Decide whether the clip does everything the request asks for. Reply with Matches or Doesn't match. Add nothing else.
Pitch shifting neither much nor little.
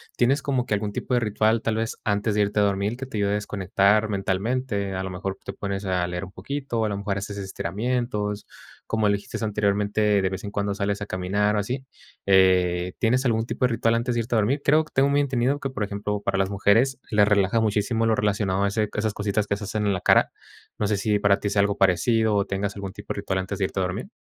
Doesn't match